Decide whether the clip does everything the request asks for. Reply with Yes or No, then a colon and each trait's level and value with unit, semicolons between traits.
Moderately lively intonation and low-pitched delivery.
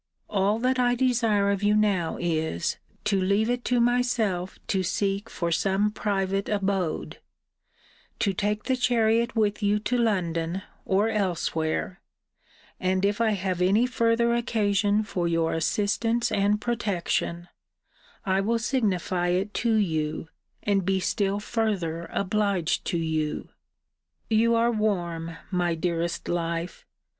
No: average, 3.8 semitones; high, 200 Hz